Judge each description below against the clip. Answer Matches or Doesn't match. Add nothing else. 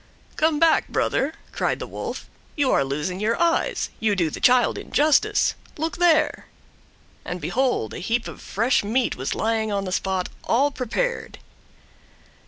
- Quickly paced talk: Doesn't match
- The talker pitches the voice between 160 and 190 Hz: Doesn't match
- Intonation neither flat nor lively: Doesn't match